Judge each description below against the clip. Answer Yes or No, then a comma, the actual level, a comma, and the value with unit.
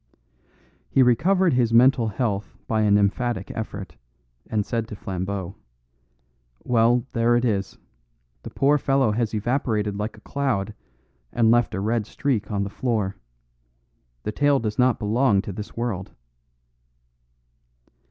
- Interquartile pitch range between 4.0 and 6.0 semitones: No, average, 3.2 semitones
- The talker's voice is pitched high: No, low, 115 Hz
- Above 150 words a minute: No, slow, 135 wpm